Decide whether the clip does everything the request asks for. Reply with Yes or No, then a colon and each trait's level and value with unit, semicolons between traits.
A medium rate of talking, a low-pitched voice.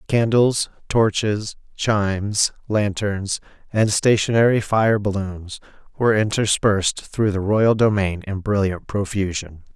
No: slow, 105 wpm; low, 105 Hz